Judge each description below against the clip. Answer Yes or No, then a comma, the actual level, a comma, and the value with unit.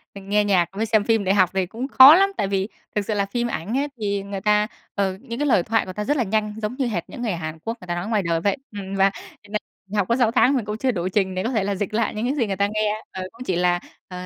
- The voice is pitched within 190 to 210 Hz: Yes, high, 205 Hz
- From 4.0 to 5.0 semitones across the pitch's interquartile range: No, average, 3.1 semitones